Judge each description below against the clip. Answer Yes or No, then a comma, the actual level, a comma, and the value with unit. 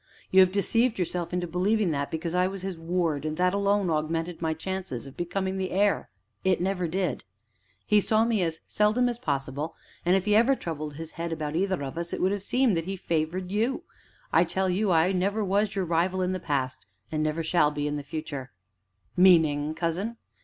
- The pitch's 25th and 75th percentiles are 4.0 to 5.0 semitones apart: No, average, 3.5 semitones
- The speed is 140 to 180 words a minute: No, fast, 205 wpm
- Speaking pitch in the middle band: Yes, medium, 180 Hz